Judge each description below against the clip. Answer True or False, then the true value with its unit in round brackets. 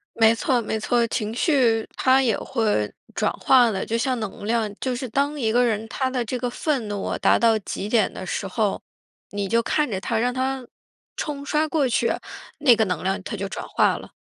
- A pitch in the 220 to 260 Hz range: True (230 Hz)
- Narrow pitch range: False (3.4 semitones)